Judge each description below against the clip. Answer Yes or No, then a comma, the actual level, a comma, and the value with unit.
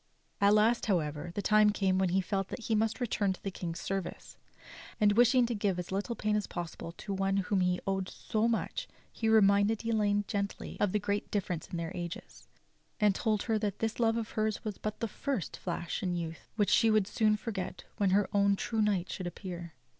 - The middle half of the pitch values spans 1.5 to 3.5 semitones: Yes, narrow, 2.6 semitones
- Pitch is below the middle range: No, high, 205 Hz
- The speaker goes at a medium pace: No, fast, 215 wpm